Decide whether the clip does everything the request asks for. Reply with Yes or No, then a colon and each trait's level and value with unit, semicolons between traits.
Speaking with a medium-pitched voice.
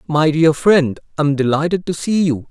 Yes: medium, 155 Hz